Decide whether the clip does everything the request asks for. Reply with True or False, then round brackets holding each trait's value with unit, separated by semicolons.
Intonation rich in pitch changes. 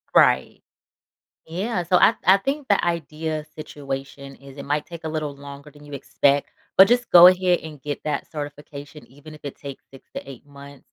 False (3.3 semitones)